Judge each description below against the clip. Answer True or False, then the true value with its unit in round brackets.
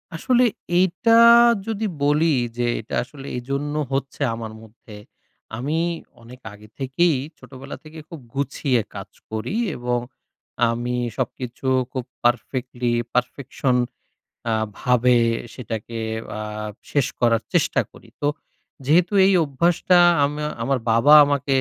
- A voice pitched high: False (135 Hz)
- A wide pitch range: False (3.7 semitones)